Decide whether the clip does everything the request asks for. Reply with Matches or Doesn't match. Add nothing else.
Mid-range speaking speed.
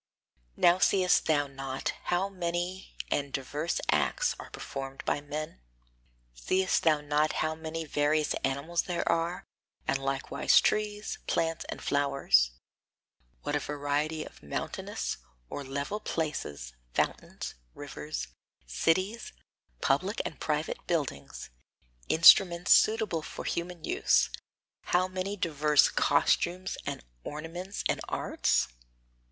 Doesn't match